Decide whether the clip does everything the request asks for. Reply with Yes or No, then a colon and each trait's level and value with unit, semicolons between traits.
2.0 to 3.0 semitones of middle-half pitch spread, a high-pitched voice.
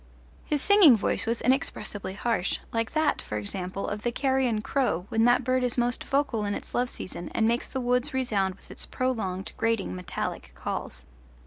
No: average, 4.1 semitones; high, 235 Hz